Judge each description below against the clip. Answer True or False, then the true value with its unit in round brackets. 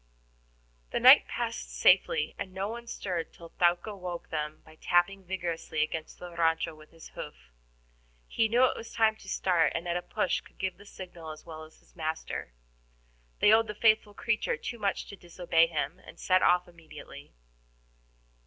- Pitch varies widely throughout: False (3.8 semitones)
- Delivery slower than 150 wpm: False (180 wpm)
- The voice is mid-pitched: True (175 Hz)